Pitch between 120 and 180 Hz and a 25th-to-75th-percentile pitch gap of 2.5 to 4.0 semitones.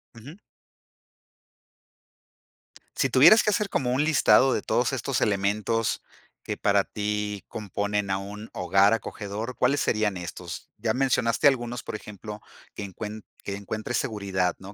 No: low, 105 Hz; average, 2.8 semitones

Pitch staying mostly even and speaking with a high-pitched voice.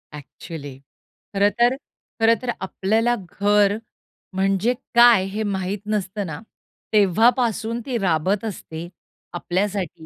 No: average, 3.3 semitones; high, 200 Hz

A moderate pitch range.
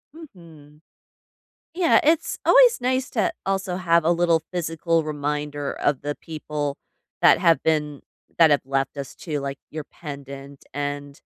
Yes: average, 3.3 semitones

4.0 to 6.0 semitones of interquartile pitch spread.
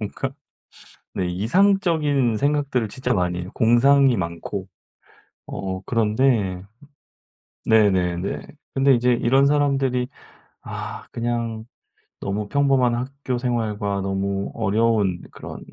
Yes: average, 5.3 semitones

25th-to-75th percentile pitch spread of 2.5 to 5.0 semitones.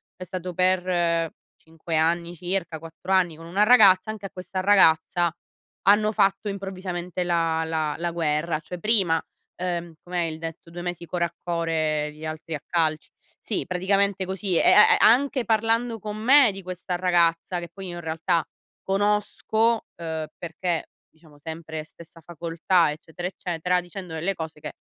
Yes: average, 2.8 semitones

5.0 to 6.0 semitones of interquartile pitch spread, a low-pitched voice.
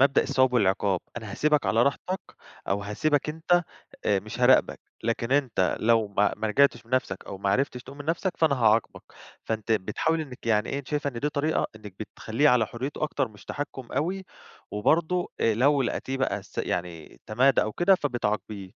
Yes: average, 5.3 semitones; low, 125 Hz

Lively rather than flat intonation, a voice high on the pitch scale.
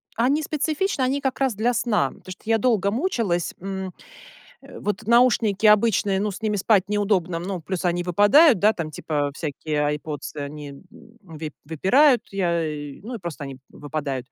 Yes: wide, 6.3 semitones; high, 195 Hz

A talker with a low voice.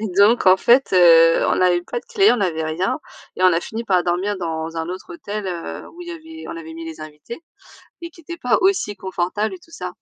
No: high, 205 Hz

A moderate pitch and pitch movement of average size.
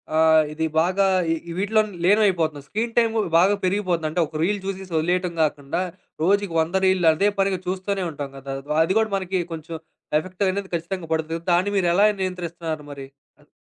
Yes: medium, 180 Hz; average, 3.4 semitones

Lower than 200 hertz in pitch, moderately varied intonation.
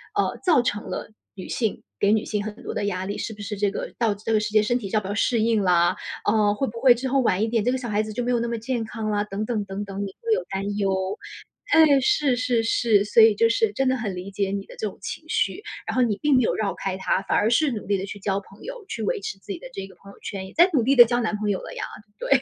No: high, 215 Hz; average, 3.2 semitones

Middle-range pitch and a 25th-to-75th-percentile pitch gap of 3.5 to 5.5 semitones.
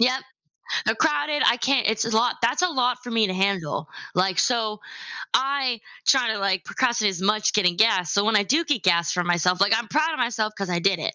No: high, 220 Hz; average, 4.8 semitones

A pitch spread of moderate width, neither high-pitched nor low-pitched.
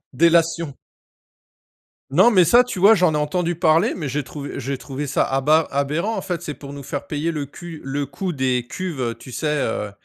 Yes: average, 3.7 semitones; medium, 150 Hz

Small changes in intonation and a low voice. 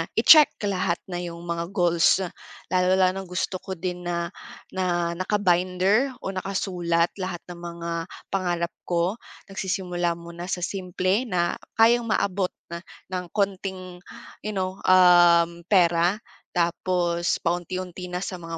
No: narrow, 1.6 semitones; medium, 180 Hz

